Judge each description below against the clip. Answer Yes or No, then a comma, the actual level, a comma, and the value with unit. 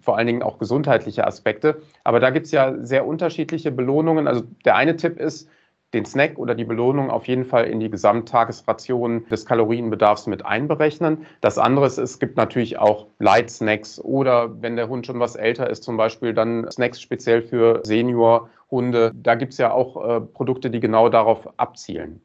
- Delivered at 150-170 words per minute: No, average, 185 wpm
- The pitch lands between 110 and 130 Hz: Yes, low, 120 Hz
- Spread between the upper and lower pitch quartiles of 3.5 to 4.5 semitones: No, average, 3.0 semitones